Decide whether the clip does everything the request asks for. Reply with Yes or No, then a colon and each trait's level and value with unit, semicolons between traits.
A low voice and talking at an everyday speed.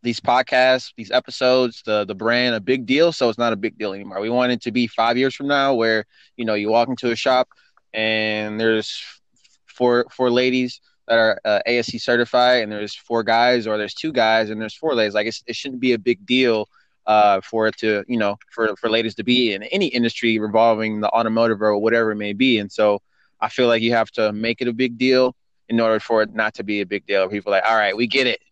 No: low, 115 Hz; fast, 250 wpm